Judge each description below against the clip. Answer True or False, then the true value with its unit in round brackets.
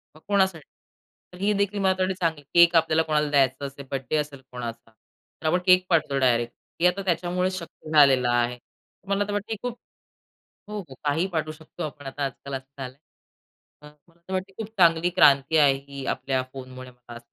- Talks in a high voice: False (155 Hz)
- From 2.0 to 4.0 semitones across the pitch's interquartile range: False (5.2 semitones)